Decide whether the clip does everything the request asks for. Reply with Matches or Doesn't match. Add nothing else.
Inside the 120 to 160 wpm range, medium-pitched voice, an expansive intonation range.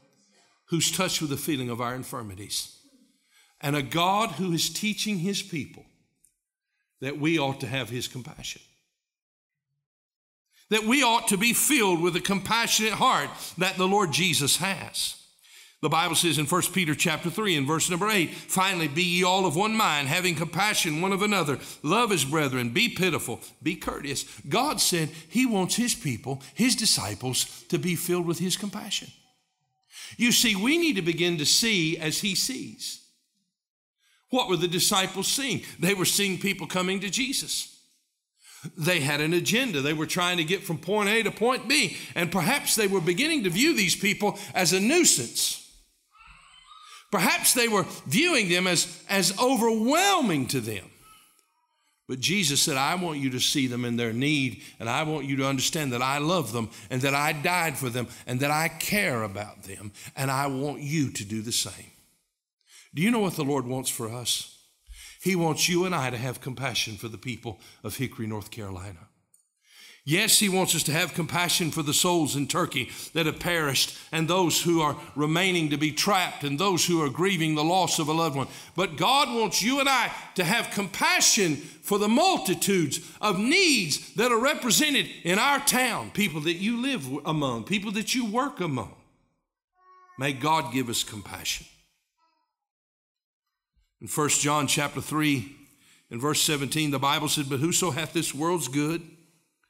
Doesn't match